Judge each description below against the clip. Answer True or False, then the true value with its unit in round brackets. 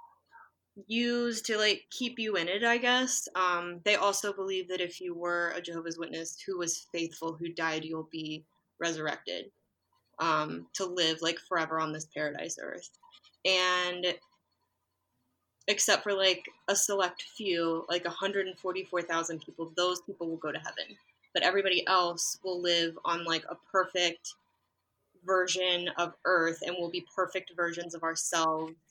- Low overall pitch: False (175 Hz)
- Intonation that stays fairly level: True (2.3 semitones)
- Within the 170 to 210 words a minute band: False (150 wpm)